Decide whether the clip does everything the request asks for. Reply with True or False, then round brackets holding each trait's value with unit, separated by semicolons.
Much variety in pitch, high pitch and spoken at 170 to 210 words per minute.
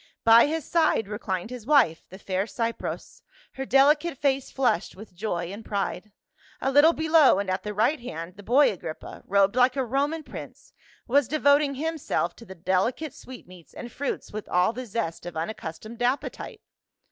True (6.4 semitones; 230 Hz; 180 wpm)